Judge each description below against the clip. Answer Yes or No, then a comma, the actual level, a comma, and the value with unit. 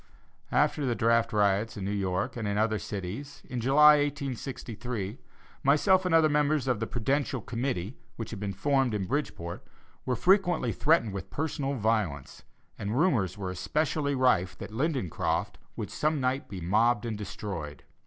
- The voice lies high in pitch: No, low, 120 Hz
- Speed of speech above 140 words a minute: Yes, average, 160 wpm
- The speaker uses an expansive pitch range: Yes, wide, 5.7 semitones